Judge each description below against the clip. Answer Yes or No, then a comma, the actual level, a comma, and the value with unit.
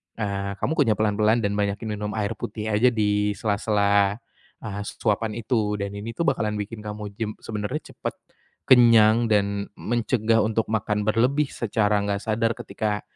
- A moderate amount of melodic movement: No, narrow, 1.7 semitones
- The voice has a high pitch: No, low, 105 Hz